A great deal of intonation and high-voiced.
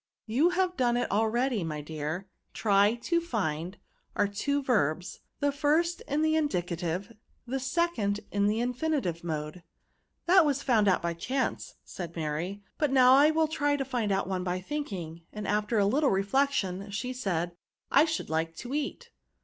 Yes: wide, 7.8 semitones; high, 215 Hz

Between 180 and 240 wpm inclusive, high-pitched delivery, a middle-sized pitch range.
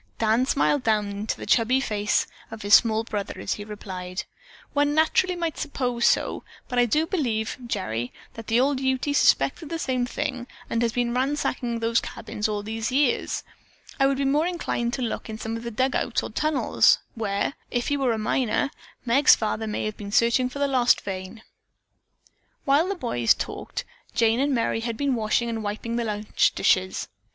Yes: average, 195 wpm; high, 235 Hz; average, 3.9 semitones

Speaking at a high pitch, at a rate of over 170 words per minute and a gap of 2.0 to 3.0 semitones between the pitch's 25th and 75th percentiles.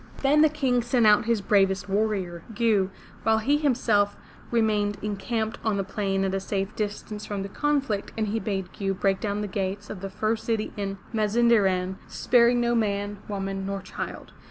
Yes: high, 210 Hz; average, 180 wpm; narrow, 2.6 semitones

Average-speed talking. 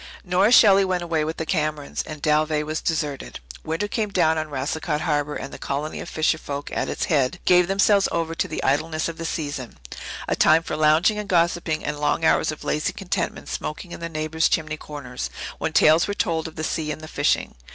No: fast, 215 wpm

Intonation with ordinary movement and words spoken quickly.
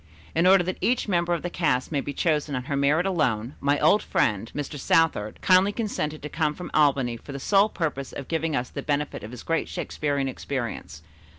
Yes: average, 4.1 semitones; fast, 210 wpm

